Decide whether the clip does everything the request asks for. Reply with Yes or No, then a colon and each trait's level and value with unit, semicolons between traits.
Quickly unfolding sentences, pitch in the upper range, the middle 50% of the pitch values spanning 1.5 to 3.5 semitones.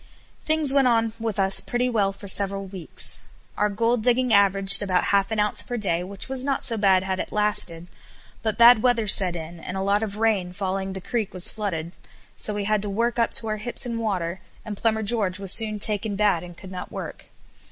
Yes: fast, 220 wpm; high, 205 Hz; average, 2.8 semitones